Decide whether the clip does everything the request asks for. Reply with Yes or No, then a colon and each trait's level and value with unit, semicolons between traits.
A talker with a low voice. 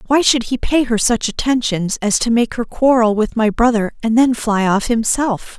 No: high, 230 Hz